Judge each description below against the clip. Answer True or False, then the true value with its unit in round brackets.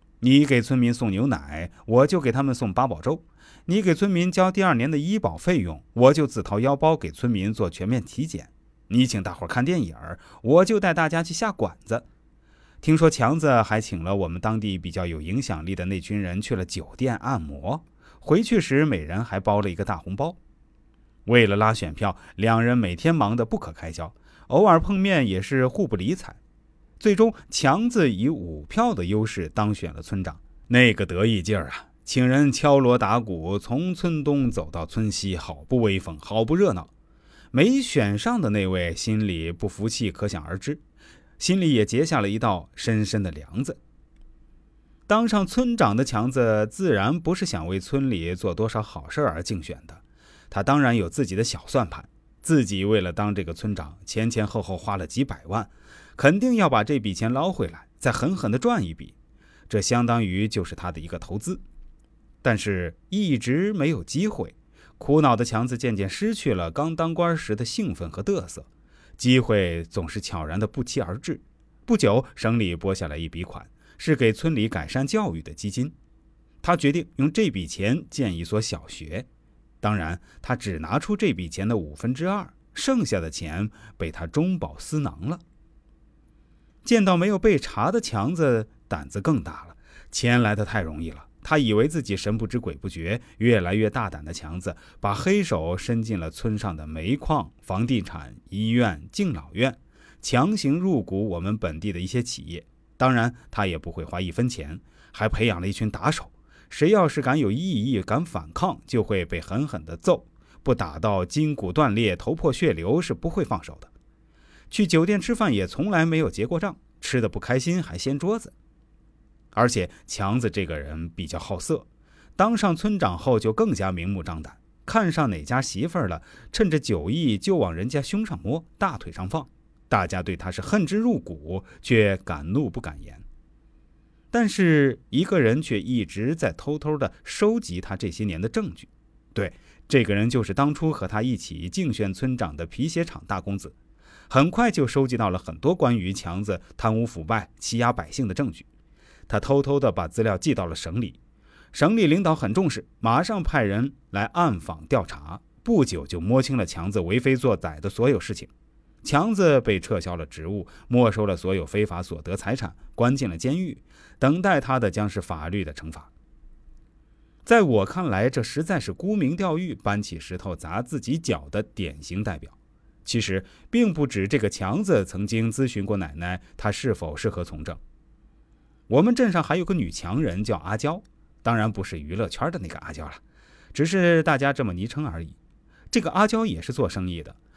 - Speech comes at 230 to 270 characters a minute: True (265 characters per minute)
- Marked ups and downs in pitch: True (7.5 semitones)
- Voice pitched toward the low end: True (110 Hz)